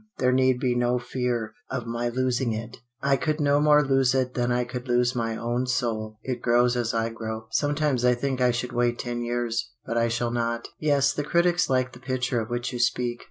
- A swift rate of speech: Yes, fast, 220 wpm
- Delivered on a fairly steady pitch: Yes, narrow, 1.5 semitones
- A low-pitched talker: Yes, low, 125 Hz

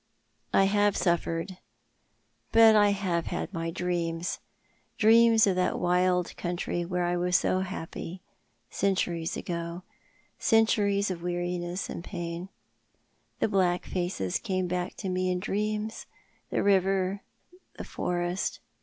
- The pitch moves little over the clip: Yes, narrow, 2.1 semitones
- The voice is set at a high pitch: No, medium, 180 Hz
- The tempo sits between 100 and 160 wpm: Yes, slow, 135 wpm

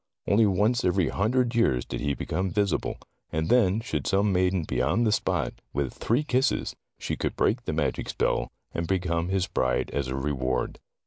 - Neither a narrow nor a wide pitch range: No, wide, 6.5 semitones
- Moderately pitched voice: No, very low, 95 Hz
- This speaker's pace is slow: No, average, 185 wpm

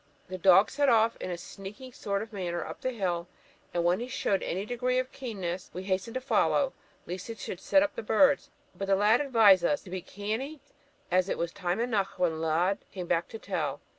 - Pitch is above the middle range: Yes, high, 200 Hz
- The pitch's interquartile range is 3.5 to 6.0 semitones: Yes, average, 4.8 semitones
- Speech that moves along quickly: Yes, fast, 220 wpm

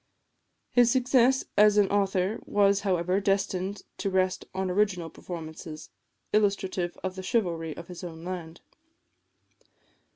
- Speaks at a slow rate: Yes, slow, 125 wpm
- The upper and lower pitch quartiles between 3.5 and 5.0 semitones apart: No, narrow, 2.6 semitones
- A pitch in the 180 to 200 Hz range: Yes, high, 190 Hz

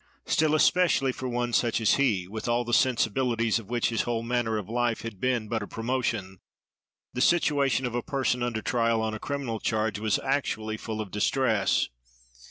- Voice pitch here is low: Yes, low, 120 Hz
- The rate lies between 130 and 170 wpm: No, average, 185 wpm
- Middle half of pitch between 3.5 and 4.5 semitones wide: No, narrow, 2.6 semitones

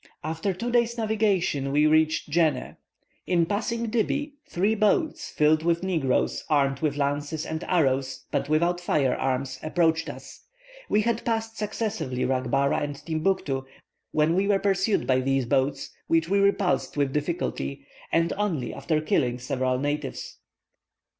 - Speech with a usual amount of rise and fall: No, wide, 6.2 semitones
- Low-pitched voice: No, medium, 160 Hz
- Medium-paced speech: Yes, average, 145 wpm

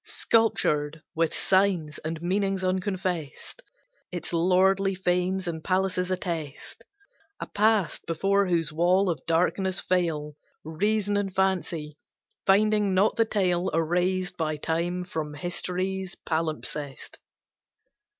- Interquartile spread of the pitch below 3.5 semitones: Yes, average, 2.8 semitones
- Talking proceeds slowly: Yes, slow, 110 wpm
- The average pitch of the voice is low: No, medium, 180 Hz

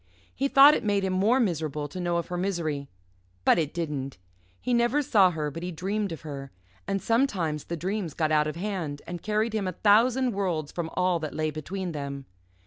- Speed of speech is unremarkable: No, fast, 210 wpm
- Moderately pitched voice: Yes, medium, 175 Hz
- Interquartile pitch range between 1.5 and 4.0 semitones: No, average, 5.0 semitones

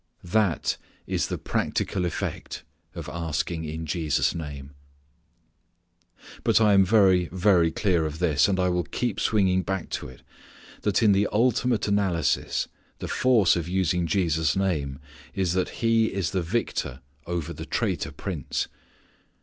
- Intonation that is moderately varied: Yes, average, 3.5 semitones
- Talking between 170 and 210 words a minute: No, average, 140 wpm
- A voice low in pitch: Yes, very low, 90 Hz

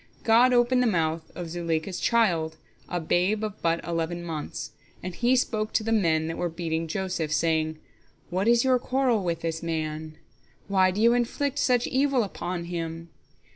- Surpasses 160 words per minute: Yes, average, 175 wpm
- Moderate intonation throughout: No, wide, 5.9 semitones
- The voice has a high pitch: No, medium, 175 Hz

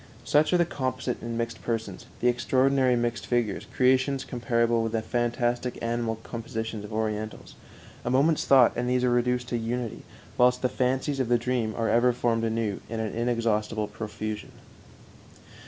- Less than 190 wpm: Yes, average, 165 wpm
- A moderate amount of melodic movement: No, narrow, 1.9 semitones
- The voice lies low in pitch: Yes, low, 120 Hz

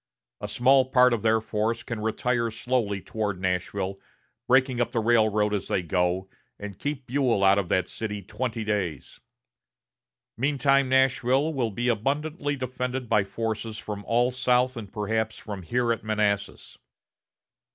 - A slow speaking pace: No, average, 150 wpm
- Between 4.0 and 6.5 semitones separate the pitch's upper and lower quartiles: No, average, 3.6 semitones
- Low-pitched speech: Yes, low, 115 Hz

